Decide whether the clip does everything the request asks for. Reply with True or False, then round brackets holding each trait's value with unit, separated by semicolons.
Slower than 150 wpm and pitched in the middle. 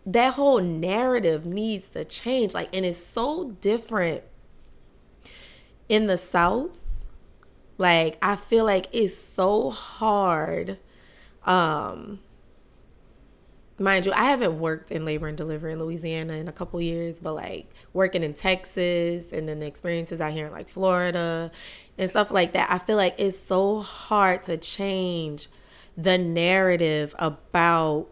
True (140 wpm; 180 Hz)